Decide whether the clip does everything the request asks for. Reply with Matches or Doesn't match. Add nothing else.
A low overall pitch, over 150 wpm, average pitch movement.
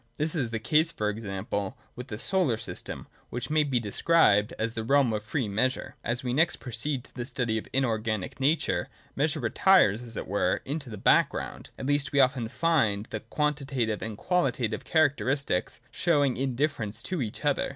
Matches